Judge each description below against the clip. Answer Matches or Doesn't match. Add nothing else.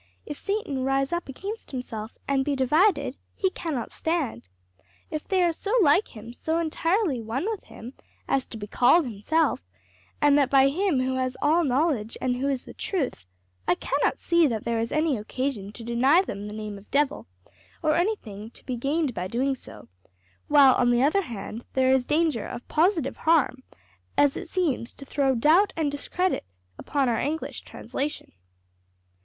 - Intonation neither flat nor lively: Matches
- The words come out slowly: Doesn't match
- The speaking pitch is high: Matches